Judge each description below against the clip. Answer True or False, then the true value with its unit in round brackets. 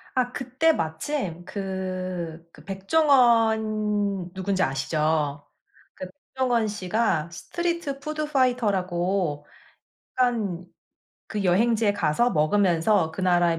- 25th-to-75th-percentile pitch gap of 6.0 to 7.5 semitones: False (5.5 semitones)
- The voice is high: True (195 Hz)